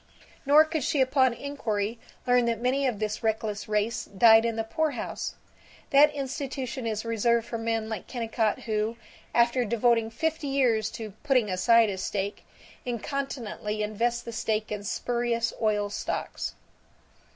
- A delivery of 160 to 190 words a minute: No, average, 145 wpm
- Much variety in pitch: No, average, 2.9 semitones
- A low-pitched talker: No, high, 230 Hz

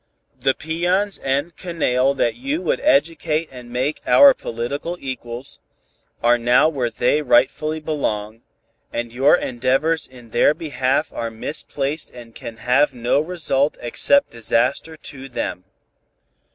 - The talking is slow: Yes, slow, 130 wpm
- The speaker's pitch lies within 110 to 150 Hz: Yes, low, 135 Hz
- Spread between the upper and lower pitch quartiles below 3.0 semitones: No, average, 4.4 semitones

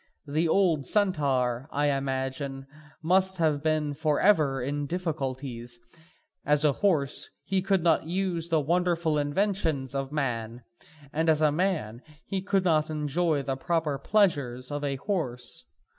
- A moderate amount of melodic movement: Yes, average, 4.1 semitones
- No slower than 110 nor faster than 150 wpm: Yes, average, 145 wpm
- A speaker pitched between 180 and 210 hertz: No, medium, 150 Hz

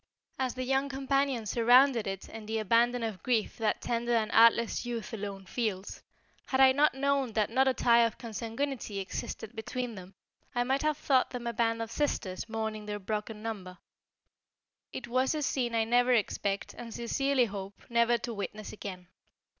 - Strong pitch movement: No, average, 3.0 semitones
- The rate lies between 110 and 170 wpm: No, average, 180 wpm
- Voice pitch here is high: Yes, high, 230 Hz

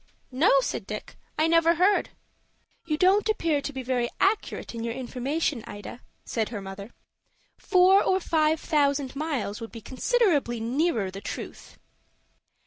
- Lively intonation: Yes, wide, 6.2 semitones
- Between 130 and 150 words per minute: Yes, average, 145 wpm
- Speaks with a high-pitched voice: Yes, very high, 285 Hz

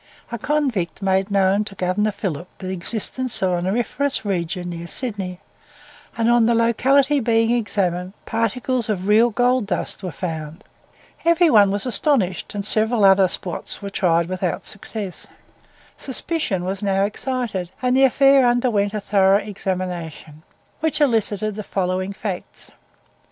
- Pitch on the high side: Yes, high, 205 Hz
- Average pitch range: Yes, average, 4.4 semitones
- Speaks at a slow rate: No, average, 145 wpm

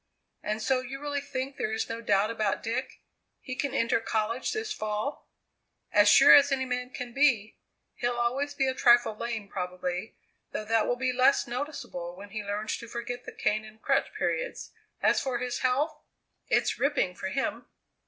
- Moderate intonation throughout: Yes, average, 3.7 semitones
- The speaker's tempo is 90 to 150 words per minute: No, average, 185 wpm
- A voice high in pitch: Yes, high, 240 Hz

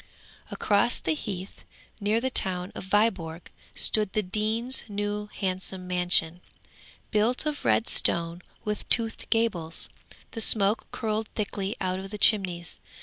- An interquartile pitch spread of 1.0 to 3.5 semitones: Yes, average, 3.1 semitones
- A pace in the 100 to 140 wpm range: Yes, slow, 135 wpm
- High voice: Yes, high, 200 Hz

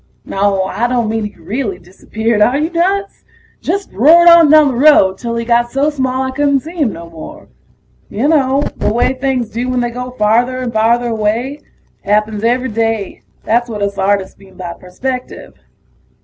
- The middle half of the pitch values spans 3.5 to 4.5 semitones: Yes, average, 4.1 semitones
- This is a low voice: No, high, 240 Hz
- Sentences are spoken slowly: No, average, 185 wpm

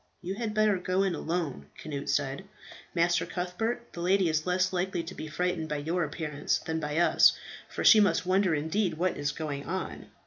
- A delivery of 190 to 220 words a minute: Yes, average, 195 wpm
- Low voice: No, medium, 175 Hz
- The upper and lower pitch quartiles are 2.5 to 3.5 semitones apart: Yes, average, 3.2 semitones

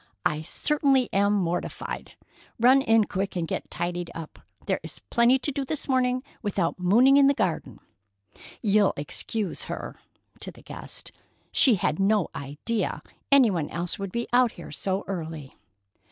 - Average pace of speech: Yes, average, 150 wpm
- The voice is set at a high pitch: Yes, high, 200 Hz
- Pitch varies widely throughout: Yes, wide, 6.3 semitones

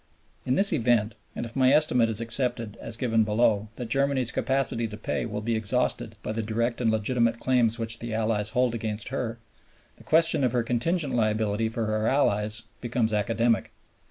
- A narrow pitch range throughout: Yes, narrow, 2.2 semitones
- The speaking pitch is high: No, low, 115 Hz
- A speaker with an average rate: Yes, average, 185 wpm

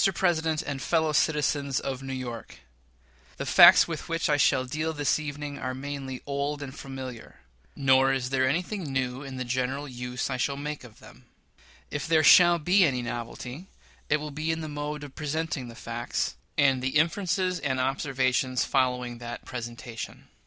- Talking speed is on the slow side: No, average, 175 wpm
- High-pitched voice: No, medium, 140 Hz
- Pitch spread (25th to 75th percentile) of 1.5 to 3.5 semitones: Yes, average, 2.8 semitones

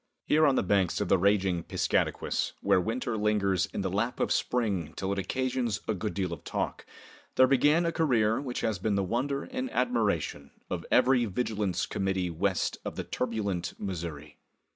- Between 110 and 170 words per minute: No, average, 180 wpm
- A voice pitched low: Yes, low, 105 Hz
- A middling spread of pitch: Yes, average, 5.0 semitones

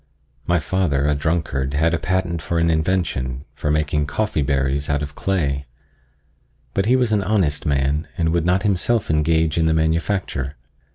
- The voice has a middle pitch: No, very low, 80 Hz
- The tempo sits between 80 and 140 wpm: No, average, 170 wpm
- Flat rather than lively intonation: No, average, 3.8 semitones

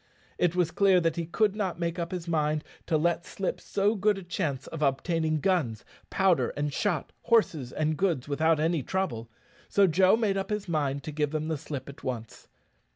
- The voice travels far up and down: No, average, 4.1 semitones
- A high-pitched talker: No, medium, 165 Hz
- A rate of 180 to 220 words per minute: Yes, average, 200 wpm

